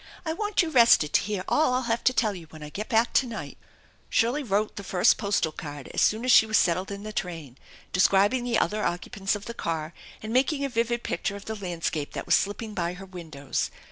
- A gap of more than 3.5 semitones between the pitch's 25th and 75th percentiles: Yes, average, 4.9 semitones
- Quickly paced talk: Yes, fast, 235 wpm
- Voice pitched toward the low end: No, high, 205 Hz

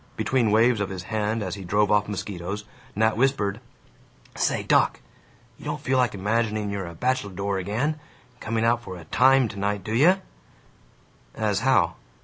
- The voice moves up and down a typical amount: Yes, average, 3.1 semitones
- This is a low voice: Yes, low, 105 Hz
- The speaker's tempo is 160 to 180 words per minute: Yes, average, 165 wpm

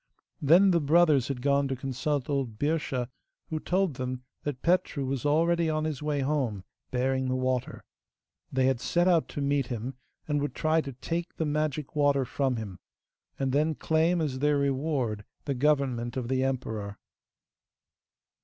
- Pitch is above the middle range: No, medium, 140 Hz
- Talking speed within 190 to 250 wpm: No, average, 165 wpm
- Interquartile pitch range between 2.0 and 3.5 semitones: Yes, average, 3.1 semitones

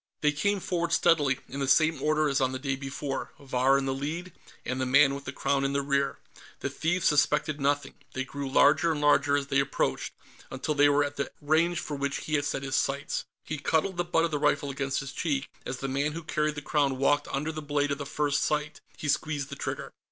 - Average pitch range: No, narrow, 1.9 semitones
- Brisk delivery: Yes, fast, 240 wpm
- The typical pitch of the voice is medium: Yes, medium, 145 Hz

